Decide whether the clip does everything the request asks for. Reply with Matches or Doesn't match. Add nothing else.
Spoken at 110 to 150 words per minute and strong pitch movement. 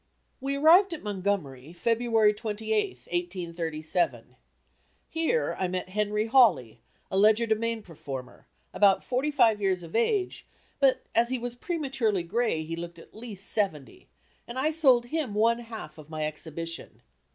Matches